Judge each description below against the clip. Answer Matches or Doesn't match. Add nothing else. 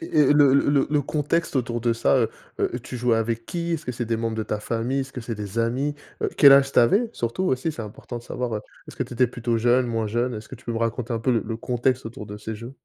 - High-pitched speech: Doesn't match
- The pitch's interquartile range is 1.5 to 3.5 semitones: Matches